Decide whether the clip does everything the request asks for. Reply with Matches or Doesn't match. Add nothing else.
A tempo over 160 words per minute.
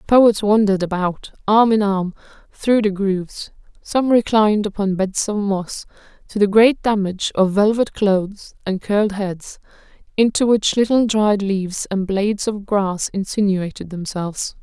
Doesn't match